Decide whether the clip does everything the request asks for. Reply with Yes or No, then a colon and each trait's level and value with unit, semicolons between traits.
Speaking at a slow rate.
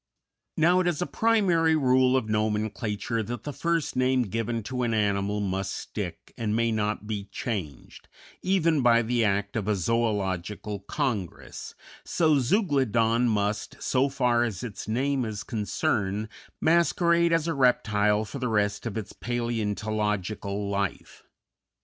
No: average, 145 wpm